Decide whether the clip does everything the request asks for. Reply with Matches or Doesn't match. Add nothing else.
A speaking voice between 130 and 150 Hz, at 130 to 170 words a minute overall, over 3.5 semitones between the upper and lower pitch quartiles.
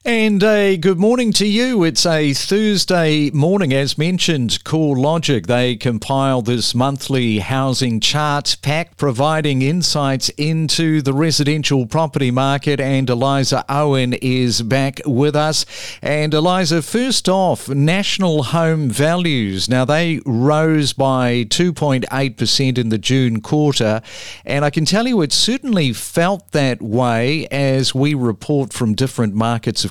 Matches